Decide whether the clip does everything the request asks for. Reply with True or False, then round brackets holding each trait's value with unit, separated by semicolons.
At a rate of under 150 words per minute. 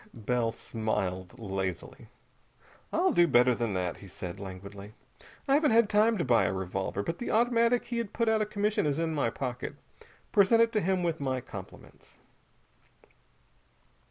False (165 wpm)